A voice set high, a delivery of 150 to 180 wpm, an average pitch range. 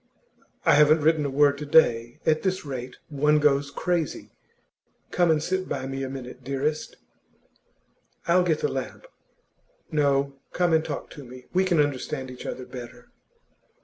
No: medium, 145 Hz; average, 160 wpm; average, 3.1 semitones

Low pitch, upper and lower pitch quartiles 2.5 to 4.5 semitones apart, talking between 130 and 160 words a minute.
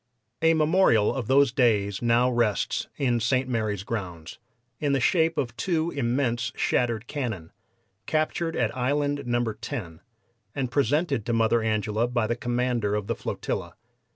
Yes: low, 120 Hz; average, 4.1 semitones; average, 150 wpm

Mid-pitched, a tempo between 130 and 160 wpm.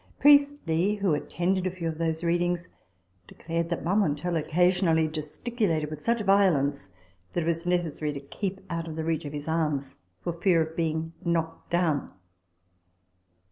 Yes: medium, 165 Hz; average, 155 wpm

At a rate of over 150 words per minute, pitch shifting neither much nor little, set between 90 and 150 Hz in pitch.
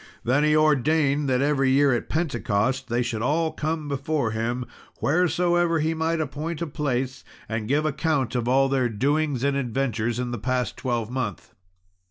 Yes: average, 165 wpm; average, 3.9 semitones; low, 135 Hz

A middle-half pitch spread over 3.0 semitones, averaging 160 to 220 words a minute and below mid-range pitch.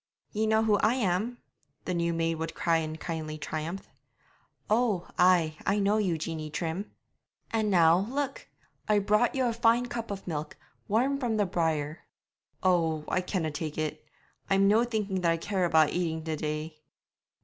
No: average, 5.0 semitones; average, 170 wpm; medium, 180 Hz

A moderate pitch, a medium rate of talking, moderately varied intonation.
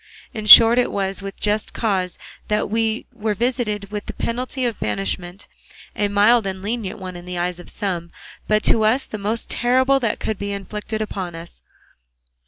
No: high, 210 Hz; average, 185 wpm; average, 3.0 semitones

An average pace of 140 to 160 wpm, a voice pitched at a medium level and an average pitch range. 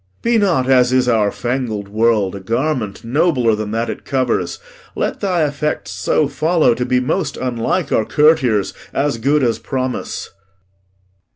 No: average, 155 wpm; low, 125 Hz; average, 4.6 semitones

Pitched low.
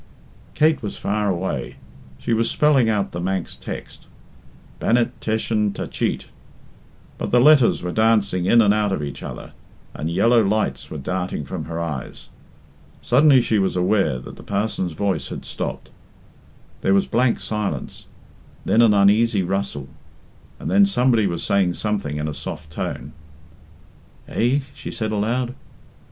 Yes: low, 100 Hz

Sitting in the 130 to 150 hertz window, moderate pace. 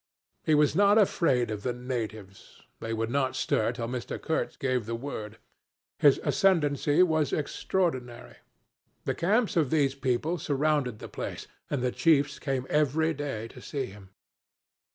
Yes: medium, 140 Hz; average, 155 wpm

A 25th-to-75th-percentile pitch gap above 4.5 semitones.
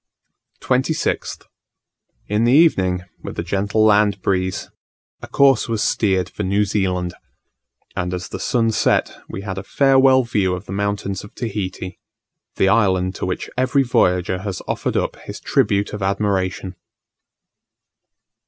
No: average, 3.2 semitones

